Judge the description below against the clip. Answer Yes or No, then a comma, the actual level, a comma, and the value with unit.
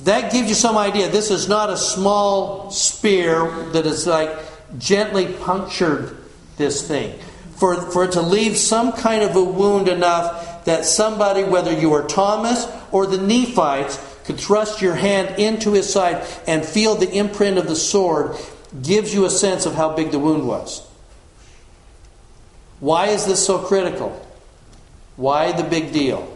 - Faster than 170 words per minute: No, average, 160 wpm